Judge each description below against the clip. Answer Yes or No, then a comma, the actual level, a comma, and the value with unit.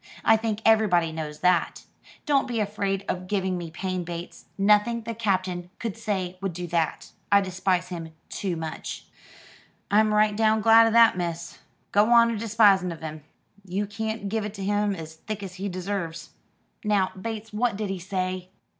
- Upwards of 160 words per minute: Yes, average, 175 wpm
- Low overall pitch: No, high, 195 Hz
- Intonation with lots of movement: No, average, 3.1 semitones